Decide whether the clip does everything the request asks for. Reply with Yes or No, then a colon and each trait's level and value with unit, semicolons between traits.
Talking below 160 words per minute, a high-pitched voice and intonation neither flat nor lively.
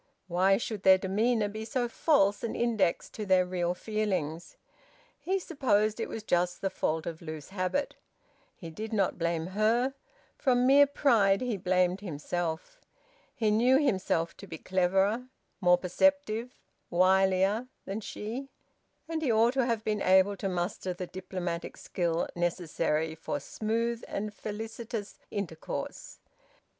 Yes: average, 140 wpm; high, 200 Hz; average, 4.3 semitones